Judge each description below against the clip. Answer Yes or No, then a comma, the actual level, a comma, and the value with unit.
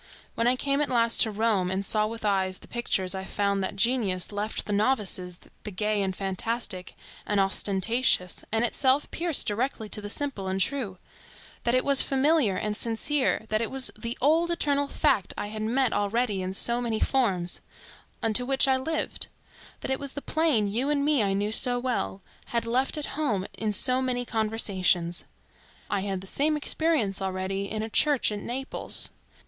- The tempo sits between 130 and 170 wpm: No, average, 180 wpm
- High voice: Yes, high, 225 Hz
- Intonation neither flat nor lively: Yes, average, 5.0 semitones